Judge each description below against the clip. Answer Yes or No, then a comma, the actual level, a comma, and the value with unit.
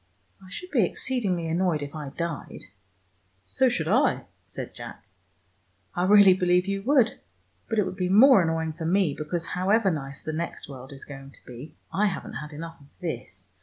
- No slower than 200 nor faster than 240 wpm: No, average, 190 wpm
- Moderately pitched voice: Yes, medium, 170 Hz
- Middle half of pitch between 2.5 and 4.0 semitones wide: No, average, 5.0 semitones